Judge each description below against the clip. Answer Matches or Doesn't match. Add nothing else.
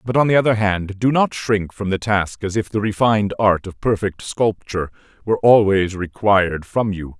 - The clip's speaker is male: Matches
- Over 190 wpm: Matches